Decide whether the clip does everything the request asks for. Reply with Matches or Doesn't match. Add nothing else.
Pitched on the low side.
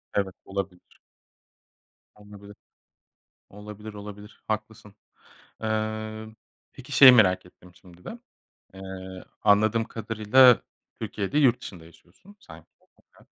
Matches